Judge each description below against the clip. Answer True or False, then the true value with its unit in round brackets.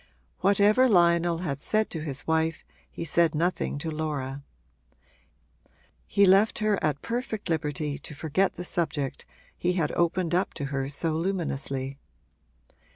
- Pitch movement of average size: True (4.0 semitones)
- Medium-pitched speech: True (165 Hz)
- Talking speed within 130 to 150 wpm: True (140 wpm)